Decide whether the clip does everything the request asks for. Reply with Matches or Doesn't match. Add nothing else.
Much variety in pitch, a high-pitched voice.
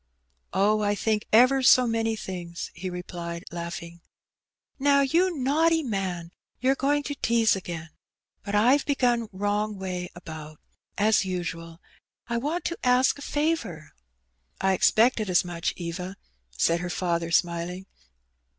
Matches